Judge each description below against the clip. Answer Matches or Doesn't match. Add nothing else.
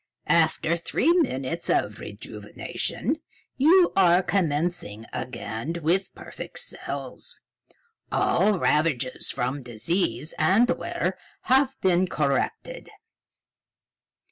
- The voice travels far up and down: Matches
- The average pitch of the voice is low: Doesn't match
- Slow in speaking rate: Matches